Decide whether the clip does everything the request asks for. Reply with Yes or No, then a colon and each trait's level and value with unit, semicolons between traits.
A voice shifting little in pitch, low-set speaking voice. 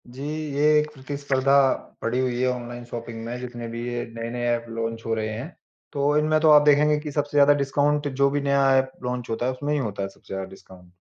No: average, 3.6 semitones; low, 125 Hz